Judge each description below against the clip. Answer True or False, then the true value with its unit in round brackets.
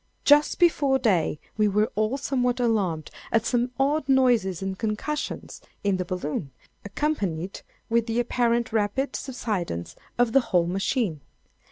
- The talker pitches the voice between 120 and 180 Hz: False (225 Hz)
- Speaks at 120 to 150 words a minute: True (140 wpm)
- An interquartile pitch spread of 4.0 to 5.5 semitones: True (5.1 semitones)